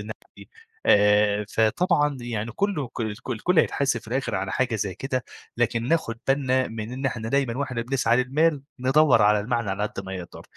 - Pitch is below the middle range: Yes, low, 120 Hz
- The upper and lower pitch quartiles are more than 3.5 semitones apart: Yes, average, 4.1 semitones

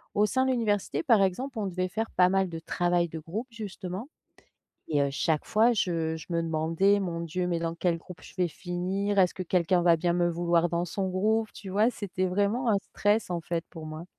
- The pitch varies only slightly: No, average, 3.3 semitones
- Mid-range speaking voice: Yes, medium, 180 Hz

